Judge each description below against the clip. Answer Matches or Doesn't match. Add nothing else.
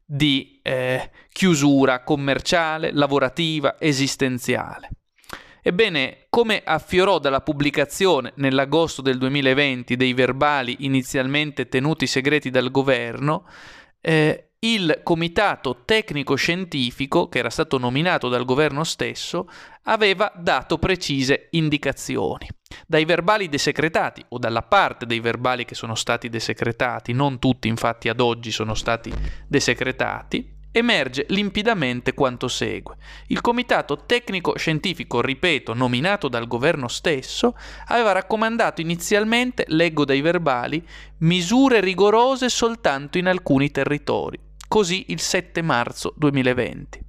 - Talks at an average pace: Doesn't match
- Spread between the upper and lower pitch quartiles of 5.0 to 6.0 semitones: Matches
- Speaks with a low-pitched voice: Doesn't match